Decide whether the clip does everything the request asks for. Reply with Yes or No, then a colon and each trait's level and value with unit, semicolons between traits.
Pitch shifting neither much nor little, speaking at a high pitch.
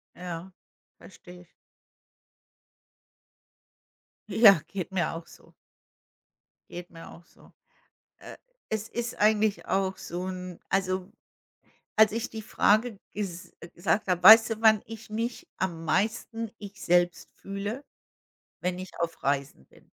Yes: average, 3.6 semitones; high, 195 Hz